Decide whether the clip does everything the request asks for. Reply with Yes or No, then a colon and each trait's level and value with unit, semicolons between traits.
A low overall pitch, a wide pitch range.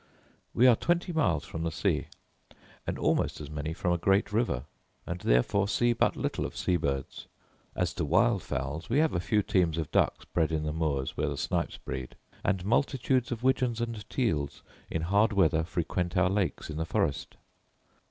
Yes: very low, 90 Hz; wide, 6.4 semitones